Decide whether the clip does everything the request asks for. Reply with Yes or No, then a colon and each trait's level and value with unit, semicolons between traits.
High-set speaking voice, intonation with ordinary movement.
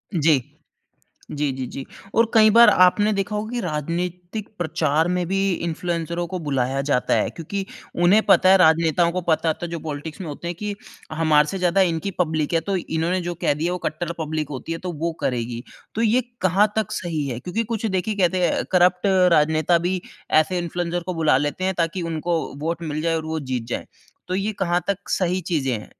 No: medium, 170 Hz; average, 3.0 semitones